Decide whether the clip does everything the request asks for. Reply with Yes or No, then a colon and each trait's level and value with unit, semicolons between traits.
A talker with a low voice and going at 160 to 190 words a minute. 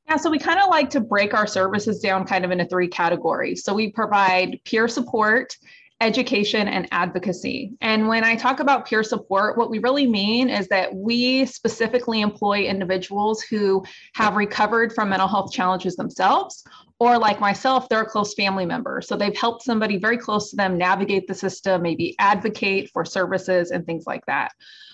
No: high, 210 Hz; average, 185 wpm